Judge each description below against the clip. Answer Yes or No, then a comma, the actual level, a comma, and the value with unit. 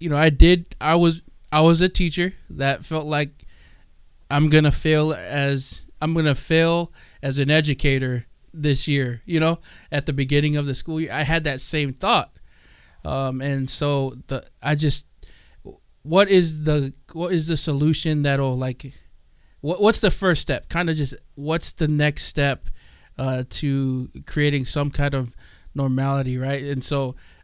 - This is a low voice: No, medium, 145 Hz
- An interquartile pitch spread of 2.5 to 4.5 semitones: Yes, average, 2.9 semitones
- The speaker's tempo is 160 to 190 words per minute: Yes, average, 165 wpm